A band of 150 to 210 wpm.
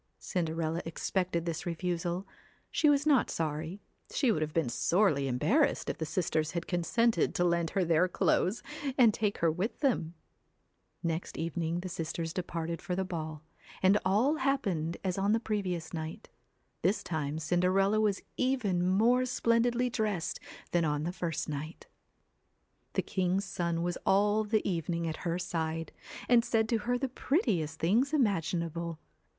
Yes: average, 155 wpm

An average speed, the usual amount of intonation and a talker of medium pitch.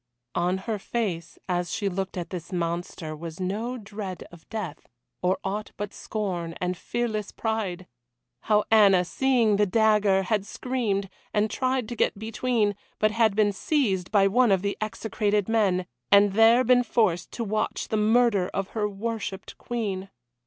No: average, 160 wpm; average, 3.0 semitones; high, 205 Hz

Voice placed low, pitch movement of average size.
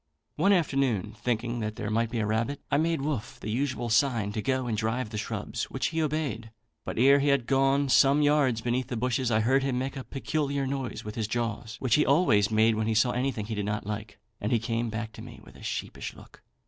Yes: low, 120 Hz; average, 3.8 semitones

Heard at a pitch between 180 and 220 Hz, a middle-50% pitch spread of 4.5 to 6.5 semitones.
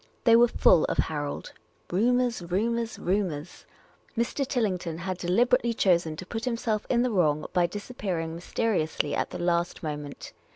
Yes: medium, 185 Hz; wide, 5.5 semitones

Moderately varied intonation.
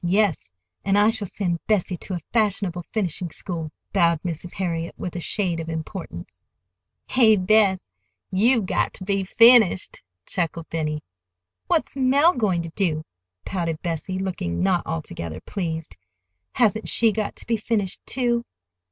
Yes: average, 4.2 semitones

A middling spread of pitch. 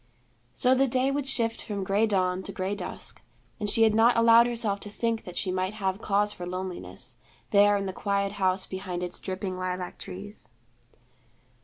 Yes: average, 3.2 semitones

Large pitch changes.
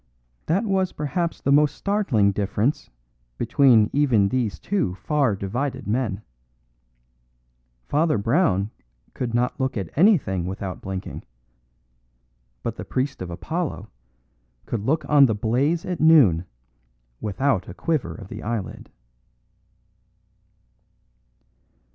Yes: wide, 7.0 semitones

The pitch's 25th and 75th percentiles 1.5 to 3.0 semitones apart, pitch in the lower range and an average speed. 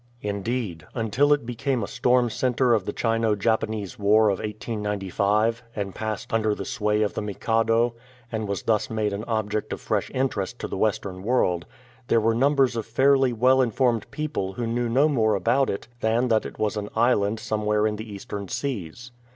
Yes: average, 2.7 semitones; low, 110 Hz; average, 190 wpm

